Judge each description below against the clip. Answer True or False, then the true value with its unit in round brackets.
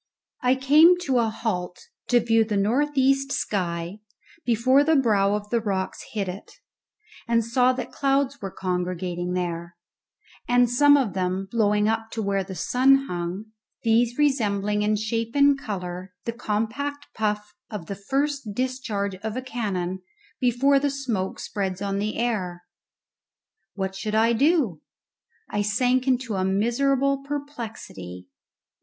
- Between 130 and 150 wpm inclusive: True (145 wpm)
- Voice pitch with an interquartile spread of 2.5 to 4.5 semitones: False (4.9 semitones)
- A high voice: True (220 Hz)